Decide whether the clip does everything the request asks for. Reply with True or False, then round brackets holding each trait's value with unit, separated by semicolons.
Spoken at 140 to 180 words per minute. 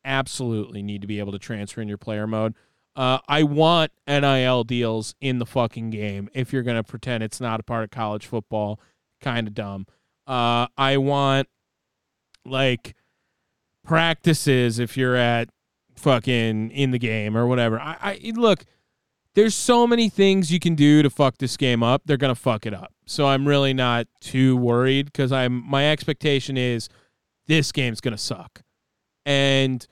True (170 wpm)